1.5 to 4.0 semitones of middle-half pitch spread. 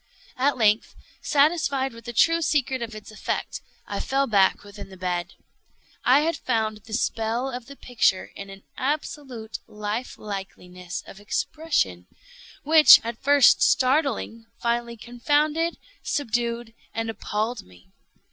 No: average, 4.7 semitones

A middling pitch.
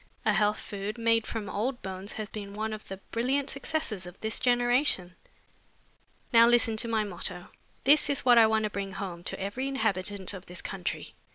No: high, 215 Hz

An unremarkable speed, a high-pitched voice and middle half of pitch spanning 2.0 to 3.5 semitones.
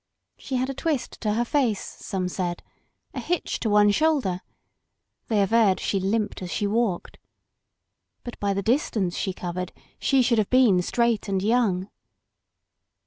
No: average, 155 wpm; high, 210 Hz; average, 4.2 semitones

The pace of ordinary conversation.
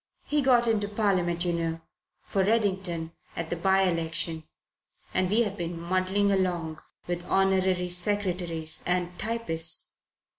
No: slow, 125 wpm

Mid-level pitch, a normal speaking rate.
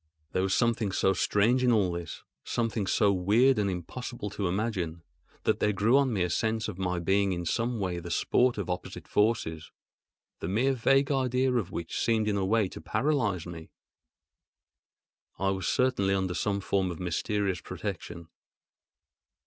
No: low, 100 Hz; average, 165 wpm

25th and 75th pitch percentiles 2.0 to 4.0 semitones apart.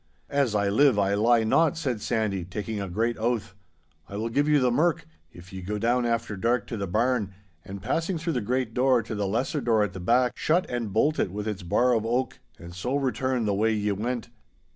Yes: average, 3.7 semitones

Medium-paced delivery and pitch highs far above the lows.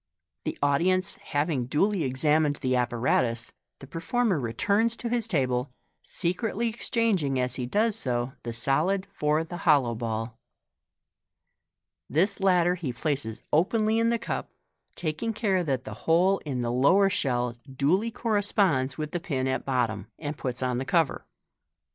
Yes: average, 155 wpm; wide, 7.2 semitones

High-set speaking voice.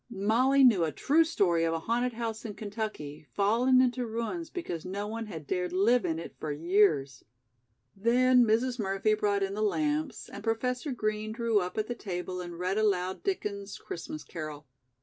Yes: high, 215 Hz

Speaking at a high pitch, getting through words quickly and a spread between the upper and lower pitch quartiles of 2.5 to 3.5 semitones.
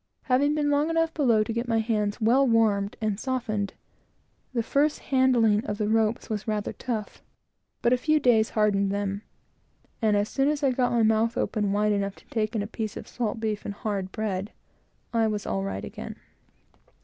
No: high, 220 Hz; average, 195 wpm; average, 3.1 semitones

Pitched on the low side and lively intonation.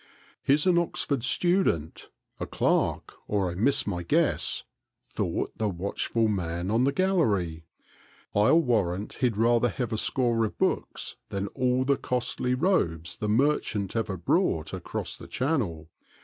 Yes: low, 115 Hz; wide, 6.1 semitones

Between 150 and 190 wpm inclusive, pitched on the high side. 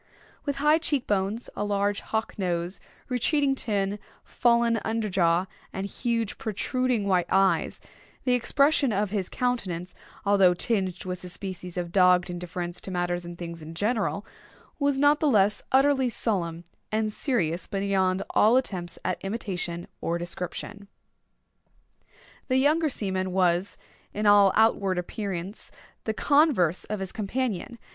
No: average, 140 wpm; high, 200 Hz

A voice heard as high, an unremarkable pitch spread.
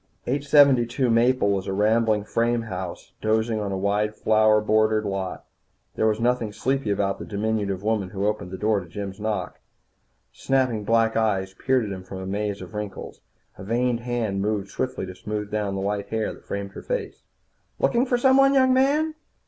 No: low, 110 Hz; average, 3.0 semitones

